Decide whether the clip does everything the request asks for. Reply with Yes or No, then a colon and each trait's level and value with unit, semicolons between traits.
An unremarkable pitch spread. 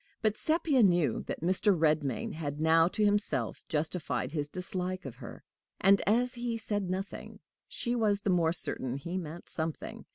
Yes: average, 4.7 semitones